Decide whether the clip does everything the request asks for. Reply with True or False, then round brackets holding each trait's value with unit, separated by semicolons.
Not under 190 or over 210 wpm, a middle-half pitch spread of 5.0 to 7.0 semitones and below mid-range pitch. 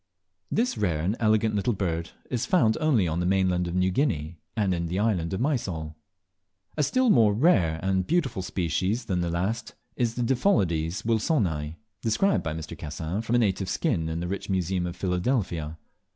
False (180 wpm; 5.3 semitones; 95 Hz)